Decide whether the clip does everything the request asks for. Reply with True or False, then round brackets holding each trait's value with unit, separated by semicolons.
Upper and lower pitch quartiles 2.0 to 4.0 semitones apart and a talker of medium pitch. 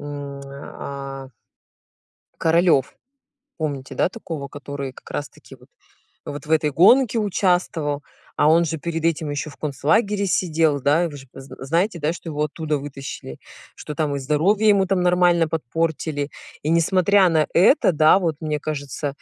True (3.5 semitones; 155 Hz)